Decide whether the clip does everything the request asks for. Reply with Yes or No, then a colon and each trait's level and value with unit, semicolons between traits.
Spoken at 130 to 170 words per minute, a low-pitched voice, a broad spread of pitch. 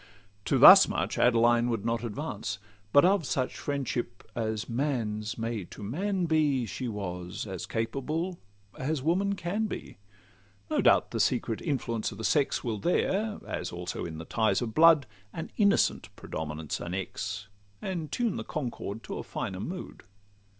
Yes: average, 155 wpm; low, 120 Hz; wide, 7.0 semitones